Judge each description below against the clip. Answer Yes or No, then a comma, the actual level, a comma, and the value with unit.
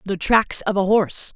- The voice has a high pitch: Yes, high, 200 Hz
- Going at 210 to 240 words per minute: Yes, fast, 220 wpm